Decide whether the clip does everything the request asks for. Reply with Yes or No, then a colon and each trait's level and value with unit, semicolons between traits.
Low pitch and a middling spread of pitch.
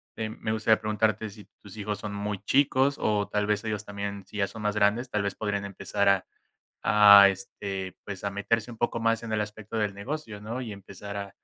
No: low, 105 Hz; narrow, 1.5 semitones